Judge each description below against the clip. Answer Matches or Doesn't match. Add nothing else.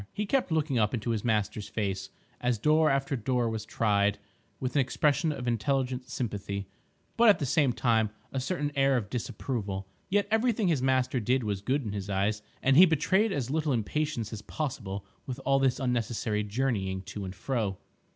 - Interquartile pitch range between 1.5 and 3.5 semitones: Doesn't match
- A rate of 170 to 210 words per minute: Matches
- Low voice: Matches